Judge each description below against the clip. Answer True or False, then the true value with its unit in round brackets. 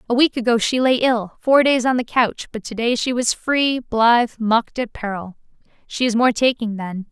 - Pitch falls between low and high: False (235 Hz)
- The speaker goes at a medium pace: False (210 wpm)